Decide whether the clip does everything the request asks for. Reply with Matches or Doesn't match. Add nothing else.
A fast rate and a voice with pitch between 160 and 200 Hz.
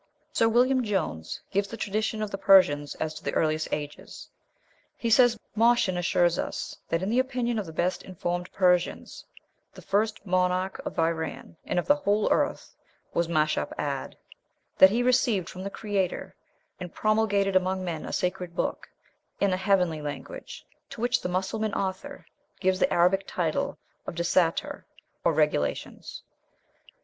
Doesn't match